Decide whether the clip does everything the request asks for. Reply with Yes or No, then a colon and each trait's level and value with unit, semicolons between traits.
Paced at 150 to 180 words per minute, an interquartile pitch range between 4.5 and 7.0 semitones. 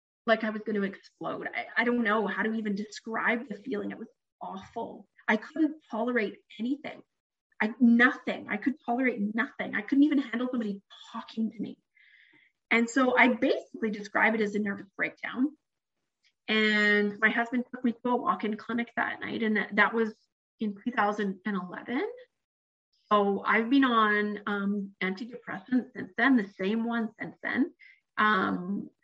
No: average, 160 wpm; average, 2.9 semitones